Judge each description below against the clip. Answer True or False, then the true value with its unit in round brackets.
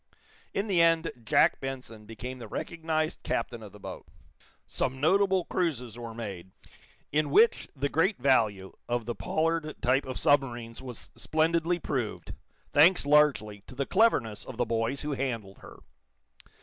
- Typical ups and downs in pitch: False (5.7 semitones)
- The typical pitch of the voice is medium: False (130 Hz)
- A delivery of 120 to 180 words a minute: True (150 wpm)